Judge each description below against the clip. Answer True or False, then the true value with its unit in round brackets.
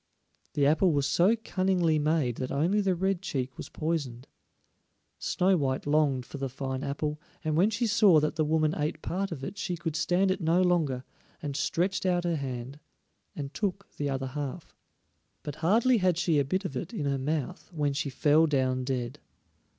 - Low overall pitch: False (155 Hz)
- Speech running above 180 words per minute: True (190 wpm)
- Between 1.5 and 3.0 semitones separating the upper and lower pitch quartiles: False (4.4 semitones)